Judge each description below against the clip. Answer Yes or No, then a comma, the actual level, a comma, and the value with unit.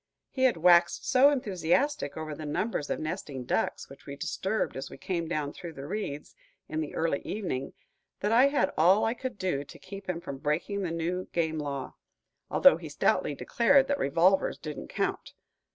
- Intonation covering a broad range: Yes, wide, 5.7 semitones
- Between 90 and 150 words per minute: No, average, 185 wpm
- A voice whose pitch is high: No, medium, 170 Hz